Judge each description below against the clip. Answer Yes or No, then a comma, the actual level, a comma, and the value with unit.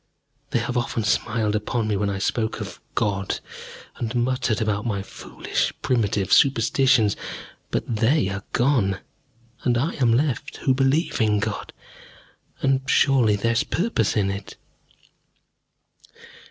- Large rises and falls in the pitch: No, average, 3.8 semitones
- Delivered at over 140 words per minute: No, slow, 135 wpm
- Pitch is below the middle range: Yes, low, 115 Hz